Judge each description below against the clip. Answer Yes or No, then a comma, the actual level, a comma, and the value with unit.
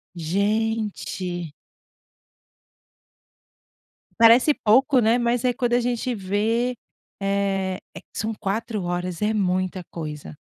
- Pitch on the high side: Yes, high, 210 Hz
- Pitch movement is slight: No, average, 4.0 semitones